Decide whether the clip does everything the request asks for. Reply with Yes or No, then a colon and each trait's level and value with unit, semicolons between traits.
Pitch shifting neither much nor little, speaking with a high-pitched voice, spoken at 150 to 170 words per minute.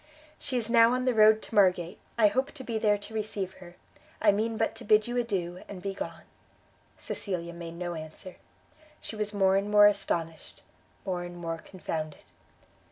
No: average, 3.7 semitones; high, 200 Hz; average, 185 wpm